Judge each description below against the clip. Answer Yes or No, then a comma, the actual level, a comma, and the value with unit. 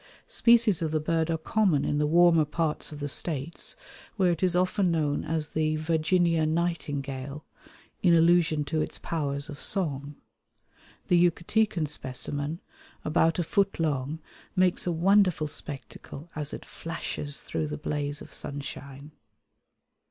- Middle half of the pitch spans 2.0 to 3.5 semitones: Yes, average, 3.1 semitones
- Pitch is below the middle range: No, medium, 160 Hz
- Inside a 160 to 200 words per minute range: No, average, 145 wpm